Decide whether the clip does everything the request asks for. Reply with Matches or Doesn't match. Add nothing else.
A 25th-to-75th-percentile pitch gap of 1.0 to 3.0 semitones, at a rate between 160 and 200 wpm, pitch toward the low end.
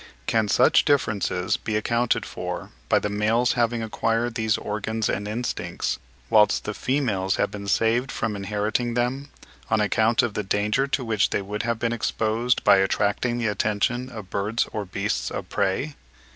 Matches